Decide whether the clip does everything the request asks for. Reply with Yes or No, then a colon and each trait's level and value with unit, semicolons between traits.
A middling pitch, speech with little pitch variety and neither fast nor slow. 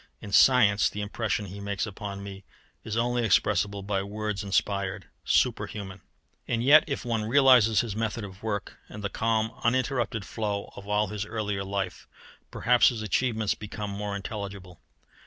No: low, 105 Hz; narrow, 2.1 semitones; average, 160 wpm